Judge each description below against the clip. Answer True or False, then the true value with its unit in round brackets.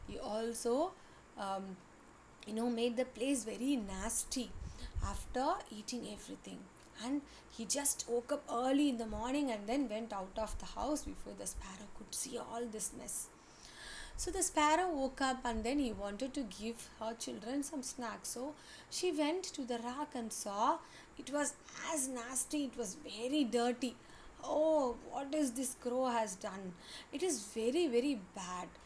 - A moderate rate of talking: True (165 wpm)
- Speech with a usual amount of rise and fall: True (3.9 semitones)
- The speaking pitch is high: True (250 Hz)